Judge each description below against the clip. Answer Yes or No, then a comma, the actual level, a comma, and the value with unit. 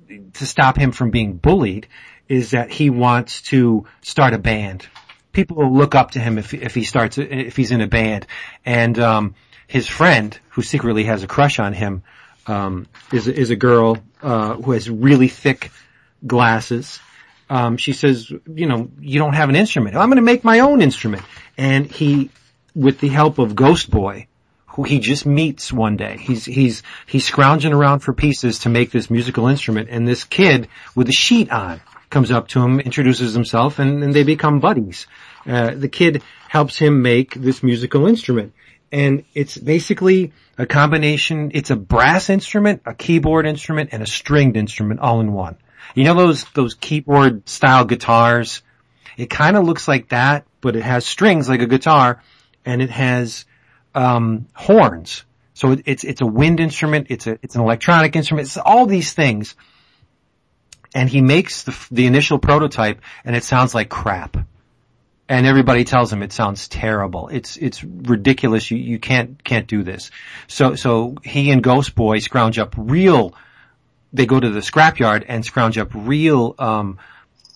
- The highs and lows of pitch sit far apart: No, average, 3.8 semitones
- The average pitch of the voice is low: Yes, low, 130 Hz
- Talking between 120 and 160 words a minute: No, average, 175 wpm